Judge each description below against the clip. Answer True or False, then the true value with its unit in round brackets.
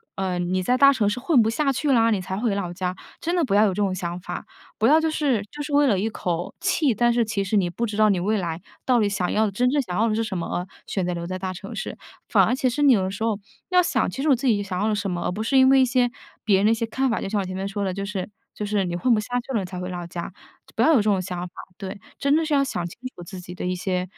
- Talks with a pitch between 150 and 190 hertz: False (210 Hz)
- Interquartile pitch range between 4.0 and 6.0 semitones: True (5.2 semitones)